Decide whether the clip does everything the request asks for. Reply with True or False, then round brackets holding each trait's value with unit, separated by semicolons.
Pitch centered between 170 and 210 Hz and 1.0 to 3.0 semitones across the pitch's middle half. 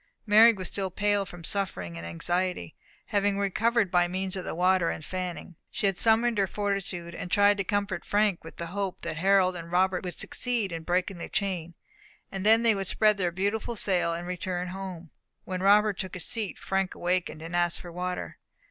True (185 Hz; 2.4 semitones)